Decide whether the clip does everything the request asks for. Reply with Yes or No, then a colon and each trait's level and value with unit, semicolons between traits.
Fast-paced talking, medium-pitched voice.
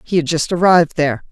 Yes: fast, 230 wpm; medium, 165 Hz